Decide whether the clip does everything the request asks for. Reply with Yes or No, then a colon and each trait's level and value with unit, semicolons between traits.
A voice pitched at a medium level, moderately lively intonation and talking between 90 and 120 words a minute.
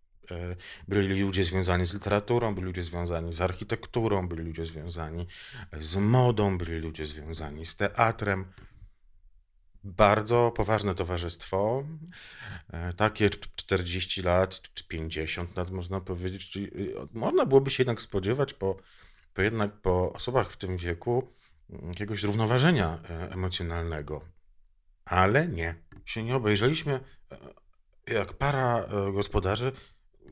No: very low, 95 Hz; average, 3.8 semitones; slow, 110 wpm